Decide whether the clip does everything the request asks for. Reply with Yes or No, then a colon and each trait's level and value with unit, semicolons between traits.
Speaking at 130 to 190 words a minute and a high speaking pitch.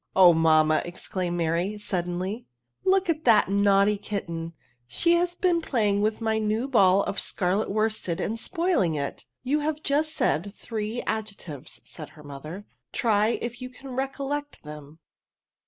Yes: average, 170 wpm; high, 210 Hz